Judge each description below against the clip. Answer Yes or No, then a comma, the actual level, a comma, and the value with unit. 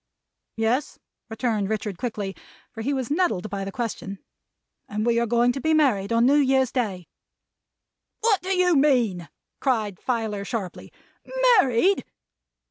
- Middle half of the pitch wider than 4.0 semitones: Yes, average, 4.7 semitones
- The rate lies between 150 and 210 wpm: No, average, 140 wpm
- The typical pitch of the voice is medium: No, high, 235 Hz